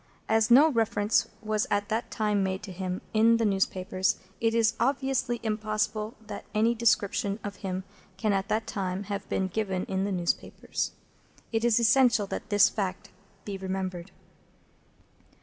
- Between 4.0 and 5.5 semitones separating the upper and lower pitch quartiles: No, average, 2.8 semitones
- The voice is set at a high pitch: Yes, high, 210 Hz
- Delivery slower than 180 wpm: Yes, average, 155 wpm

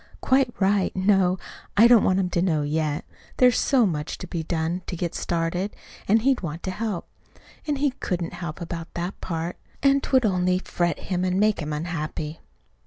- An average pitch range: Yes, average, 4.0 semitones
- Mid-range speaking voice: Yes, medium, 180 Hz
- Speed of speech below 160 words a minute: No, average, 185 wpm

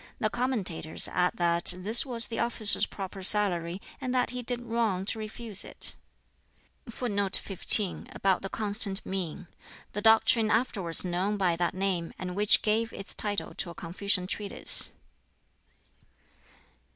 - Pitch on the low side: No, high, 200 Hz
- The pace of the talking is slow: Yes, slow, 125 wpm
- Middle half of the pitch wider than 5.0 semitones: No, average, 3.4 semitones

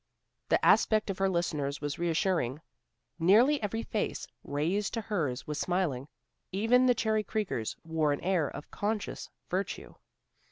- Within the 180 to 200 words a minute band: No, average, 145 wpm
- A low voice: No, medium, 185 Hz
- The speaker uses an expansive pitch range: Yes, wide, 5.9 semitones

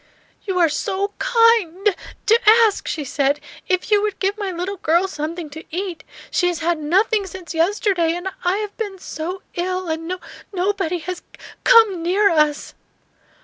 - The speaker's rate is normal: Yes, average, 175 wpm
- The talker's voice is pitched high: Yes, very high, 365 Hz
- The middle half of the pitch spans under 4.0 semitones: Yes, average, 3.3 semitones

